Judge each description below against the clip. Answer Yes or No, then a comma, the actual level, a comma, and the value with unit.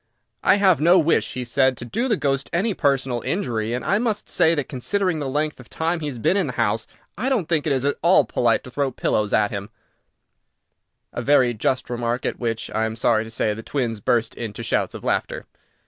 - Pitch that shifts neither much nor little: No, wide, 5.9 semitones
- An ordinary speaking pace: No, fast, 225 wpm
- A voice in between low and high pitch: No, low, 130 Hz